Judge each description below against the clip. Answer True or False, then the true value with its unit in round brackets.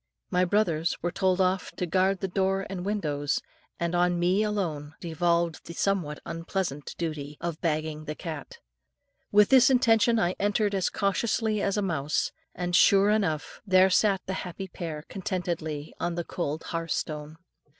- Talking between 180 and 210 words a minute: False (160 wpm)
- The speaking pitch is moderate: True (180 Hz)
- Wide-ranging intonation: False (3.6 semitones)